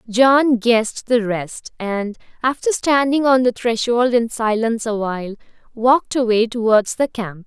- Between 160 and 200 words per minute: No, average, 145 wpm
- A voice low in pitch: No, high, 235 Hz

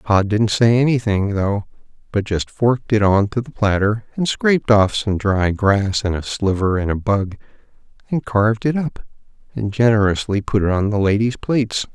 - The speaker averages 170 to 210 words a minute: Yes, average, 185 wpm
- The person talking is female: No, male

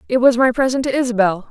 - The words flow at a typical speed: No, fast, 240 wpm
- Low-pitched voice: No, high, 245 Hz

